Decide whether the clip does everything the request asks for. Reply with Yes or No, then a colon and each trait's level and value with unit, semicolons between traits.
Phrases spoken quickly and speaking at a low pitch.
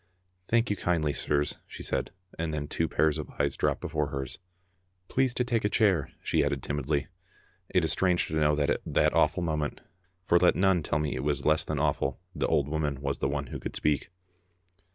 Yes: fast, 210 wpm; very low, 75 Hz